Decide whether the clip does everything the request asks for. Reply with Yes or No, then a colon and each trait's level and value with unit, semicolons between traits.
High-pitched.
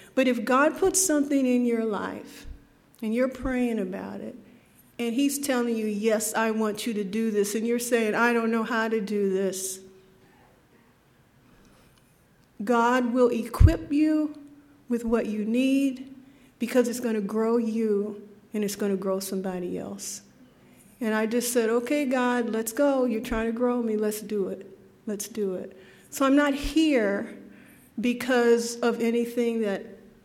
Yes: high, 230 Hz